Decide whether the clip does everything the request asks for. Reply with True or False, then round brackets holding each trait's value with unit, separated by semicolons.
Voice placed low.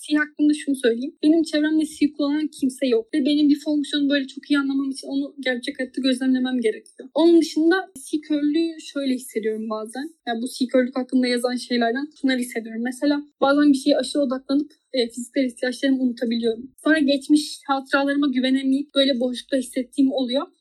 False (275 Hz)